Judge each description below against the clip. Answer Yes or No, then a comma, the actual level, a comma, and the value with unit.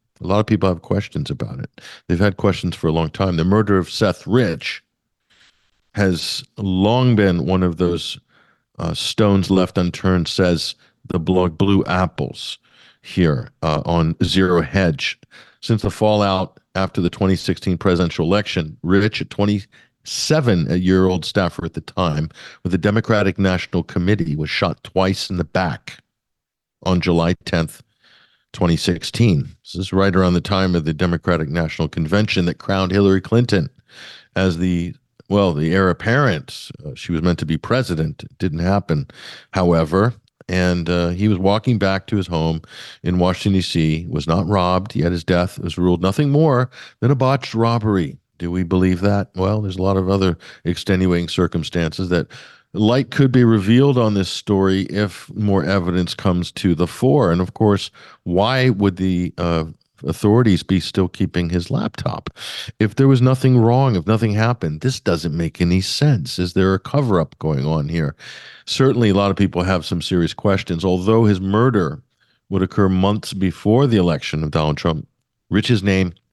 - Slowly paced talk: No, average, 170 wpm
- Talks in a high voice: No, very low, 95 Hz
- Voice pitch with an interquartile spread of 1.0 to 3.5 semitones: Yes, average, 3.1 semitones